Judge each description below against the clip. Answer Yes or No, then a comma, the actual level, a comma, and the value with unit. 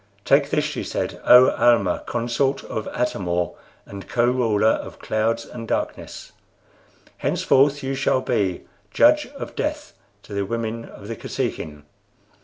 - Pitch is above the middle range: No, low, 115 Hz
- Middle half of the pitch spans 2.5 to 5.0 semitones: Yes, average, 3.9 semitones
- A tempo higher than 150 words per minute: No, average, 145 wpm